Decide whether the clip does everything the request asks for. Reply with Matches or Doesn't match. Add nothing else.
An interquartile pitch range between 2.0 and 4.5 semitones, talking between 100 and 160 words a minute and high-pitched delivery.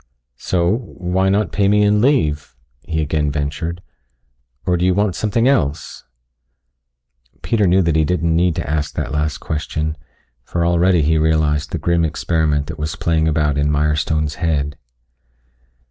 Doesn't match